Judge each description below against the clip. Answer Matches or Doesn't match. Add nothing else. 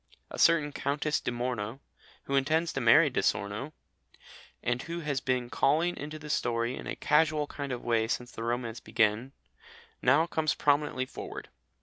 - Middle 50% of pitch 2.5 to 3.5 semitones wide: Doesn't match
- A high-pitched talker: Doesn't match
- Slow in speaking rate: Doesn't match